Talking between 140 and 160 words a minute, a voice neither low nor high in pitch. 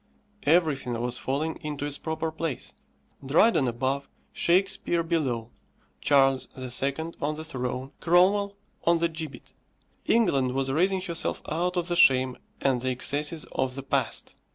Yes: average, 145 wpm; medium, 145 Hz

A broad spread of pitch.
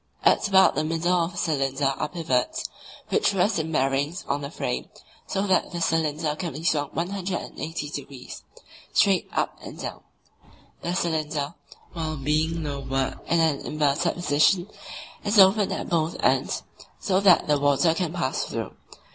No: average, 3.4 semitones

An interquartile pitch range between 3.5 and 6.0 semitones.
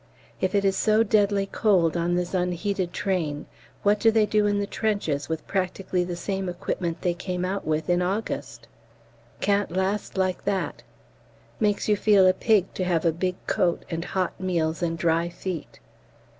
No: average, 2.7 semitones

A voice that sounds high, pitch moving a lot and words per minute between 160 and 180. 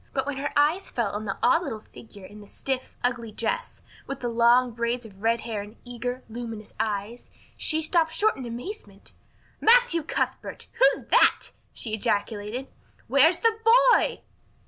Yes: high, 245 Hz; wide, 6.3 semitones; average, 170 wpm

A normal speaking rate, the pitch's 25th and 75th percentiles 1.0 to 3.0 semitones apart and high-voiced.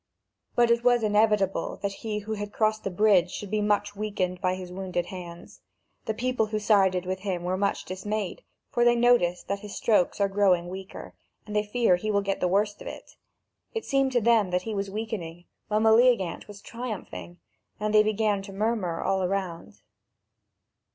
Yes: average, 190 wpm; narrow, 2.6 semitones; high, 205 Hz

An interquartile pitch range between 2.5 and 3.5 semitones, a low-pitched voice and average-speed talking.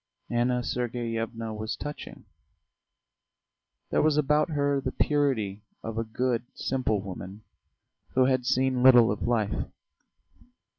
No: average, 3.0 semitones; low, 120 Hz; slow, 115 wpm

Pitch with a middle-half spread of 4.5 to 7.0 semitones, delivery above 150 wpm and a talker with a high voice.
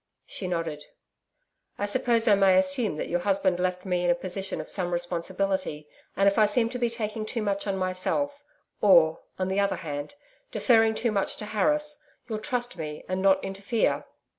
No: average, 3.7 semitones; average, 190 wpm; high, 195 Hz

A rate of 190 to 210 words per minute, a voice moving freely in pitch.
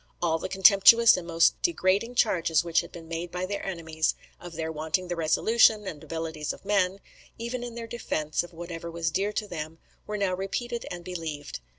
No: average, 195 wpm; average, 3.9 semitones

